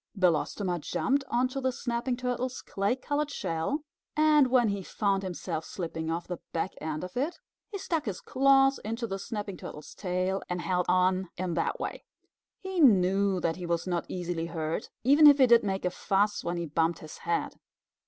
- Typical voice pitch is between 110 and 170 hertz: No, high, 195 Hz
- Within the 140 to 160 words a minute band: No, average, 185 wpm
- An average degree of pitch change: No, wide, 6.5 semitones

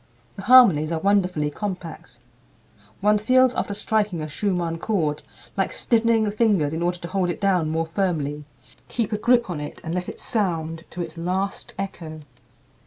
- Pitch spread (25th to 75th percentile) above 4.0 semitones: Yes, average, 4.4 semitones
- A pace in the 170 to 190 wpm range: Yes, average, 175 wpm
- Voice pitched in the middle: Yes, medium, 180 Hz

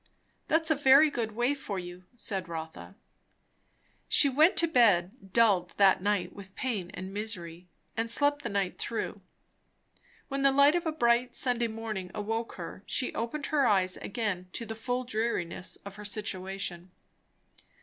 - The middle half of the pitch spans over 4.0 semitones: Yes, average, 5.1 semitones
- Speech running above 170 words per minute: No, average, 160 wpm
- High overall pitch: Yes, high, 220 Hz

